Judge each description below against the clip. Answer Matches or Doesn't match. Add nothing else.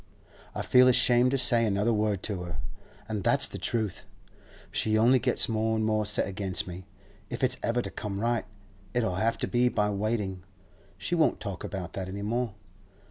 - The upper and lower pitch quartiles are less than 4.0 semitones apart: Matches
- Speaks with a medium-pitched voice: Doesn't match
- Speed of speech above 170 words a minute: Matches